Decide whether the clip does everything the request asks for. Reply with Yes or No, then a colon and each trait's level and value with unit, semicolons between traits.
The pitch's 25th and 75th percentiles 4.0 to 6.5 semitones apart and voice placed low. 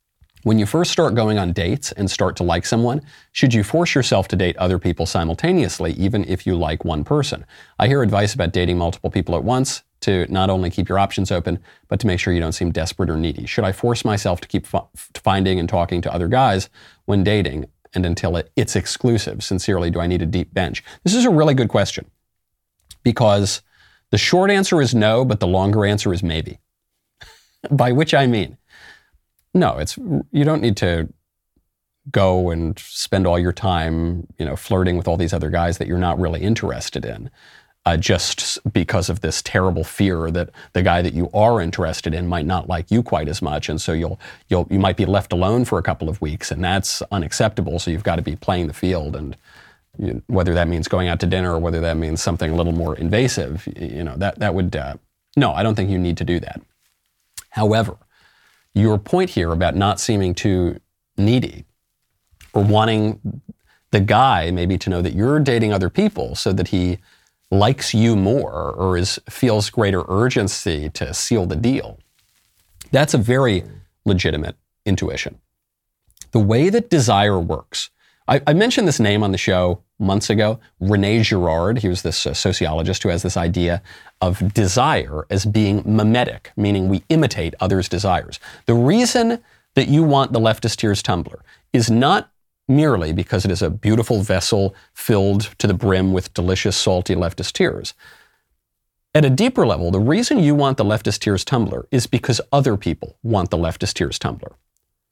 Yes: average, 4.3 semitones; very low, 95 Hz